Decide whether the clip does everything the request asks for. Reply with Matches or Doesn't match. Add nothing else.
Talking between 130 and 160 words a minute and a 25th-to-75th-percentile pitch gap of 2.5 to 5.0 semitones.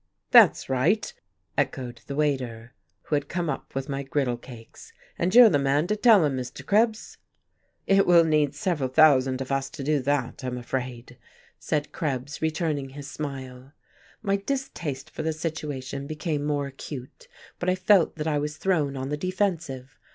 Doesn't match